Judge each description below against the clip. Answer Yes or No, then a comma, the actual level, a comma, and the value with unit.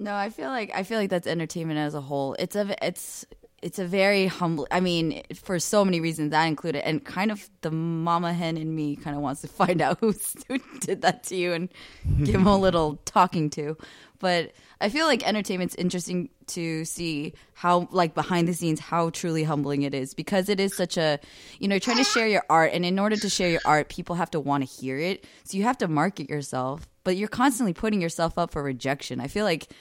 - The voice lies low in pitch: No, medium, 170 Hz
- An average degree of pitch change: Yes, average, 3.9 semitones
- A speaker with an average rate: No, fast, 230 wpm